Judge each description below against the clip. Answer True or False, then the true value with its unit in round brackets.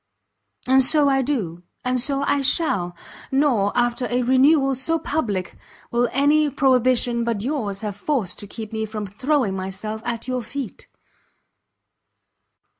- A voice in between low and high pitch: False (245 Hz)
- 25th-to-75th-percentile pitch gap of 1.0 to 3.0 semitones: False (4.5 semitones)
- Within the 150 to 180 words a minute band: False (140 wpm)